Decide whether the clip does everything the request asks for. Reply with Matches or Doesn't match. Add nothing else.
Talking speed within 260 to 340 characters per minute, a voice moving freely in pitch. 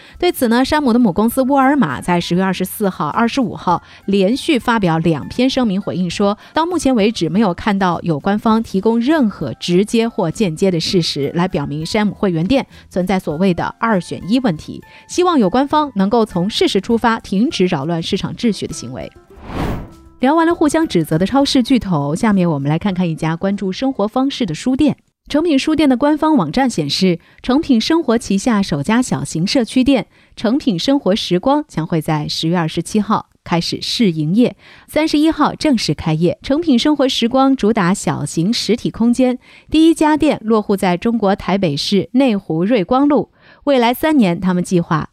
Matches